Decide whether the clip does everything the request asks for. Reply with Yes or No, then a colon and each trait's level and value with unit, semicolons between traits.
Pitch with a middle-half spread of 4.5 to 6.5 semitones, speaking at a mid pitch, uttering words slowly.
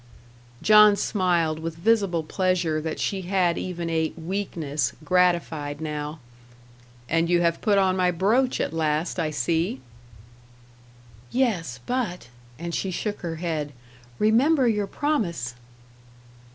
No: average, 3.9 semitones; medium, 170 Hz; slow, 125 wpm